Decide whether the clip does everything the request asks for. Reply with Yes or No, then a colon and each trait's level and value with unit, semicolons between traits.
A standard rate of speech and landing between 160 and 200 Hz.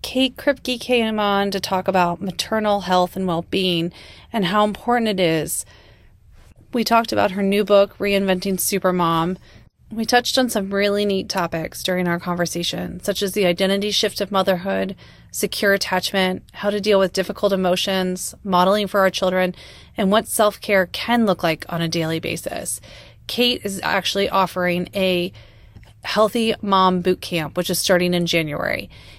Yes: average, 160 wpm; high, 190 Hz